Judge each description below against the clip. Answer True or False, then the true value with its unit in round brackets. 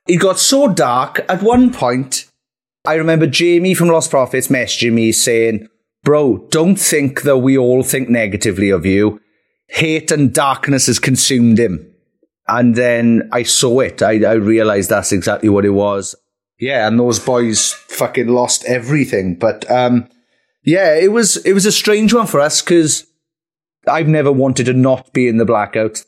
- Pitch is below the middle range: True (125 Hz)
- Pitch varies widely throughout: True (5.8 semitones)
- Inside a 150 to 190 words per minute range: True (170 wpm)